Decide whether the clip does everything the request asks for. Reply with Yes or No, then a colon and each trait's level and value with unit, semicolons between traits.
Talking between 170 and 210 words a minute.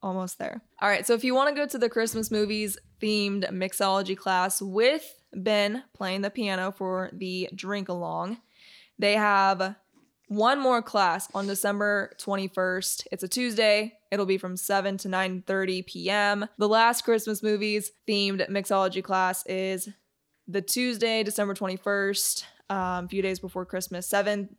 No: average, 155 wpm